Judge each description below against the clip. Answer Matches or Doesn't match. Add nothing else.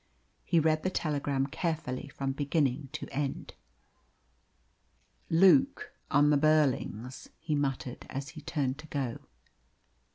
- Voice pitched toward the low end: Doesn't match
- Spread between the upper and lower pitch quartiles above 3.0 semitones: Doesn't match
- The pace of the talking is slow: Matches